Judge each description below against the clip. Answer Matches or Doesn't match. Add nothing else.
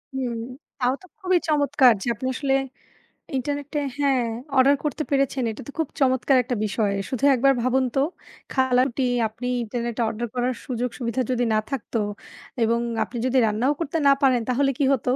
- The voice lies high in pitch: Matches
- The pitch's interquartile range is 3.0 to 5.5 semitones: Doesn't match